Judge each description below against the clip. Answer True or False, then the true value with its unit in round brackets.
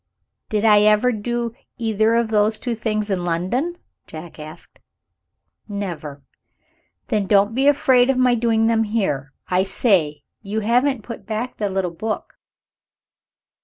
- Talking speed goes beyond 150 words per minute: False (140 wpm)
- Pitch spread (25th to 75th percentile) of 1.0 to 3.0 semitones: False (3.4 semitones)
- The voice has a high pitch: True (215 Hz)